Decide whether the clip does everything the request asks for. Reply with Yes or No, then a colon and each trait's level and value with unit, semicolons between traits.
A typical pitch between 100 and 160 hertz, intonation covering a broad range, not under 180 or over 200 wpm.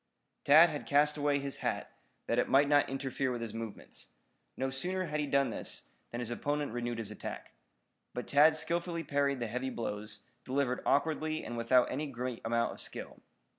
No: low, 135 Hz; average, 3.6 semitones; average, 185 wpm